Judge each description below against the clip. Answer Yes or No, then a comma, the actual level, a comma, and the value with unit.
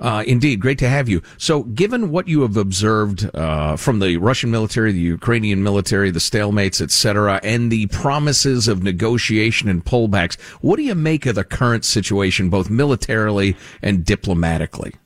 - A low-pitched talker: Yes, low, 105 Hz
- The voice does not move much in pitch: No, average, 4.1 semitones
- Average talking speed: Yes, average, 170 wpm